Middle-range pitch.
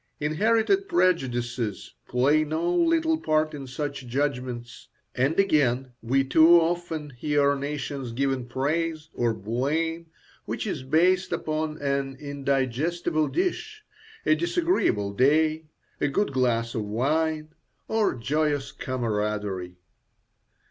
Yes: medium, 145 Hz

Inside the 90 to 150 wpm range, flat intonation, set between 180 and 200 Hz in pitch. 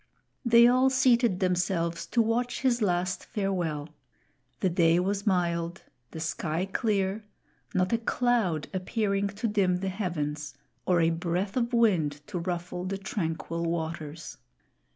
No: slow, 135 wpm; average, 4.2 semitones; medium, 185 Hz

